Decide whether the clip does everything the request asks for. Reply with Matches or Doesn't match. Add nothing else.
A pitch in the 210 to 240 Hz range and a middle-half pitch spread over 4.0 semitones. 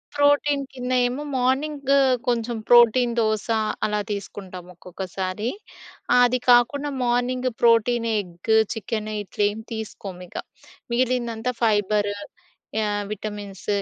Doesn't match